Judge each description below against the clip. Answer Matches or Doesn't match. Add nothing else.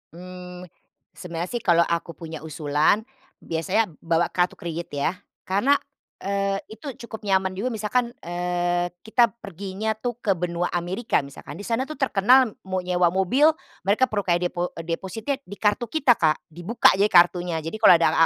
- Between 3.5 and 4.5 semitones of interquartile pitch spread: Matches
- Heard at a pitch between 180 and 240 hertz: Matches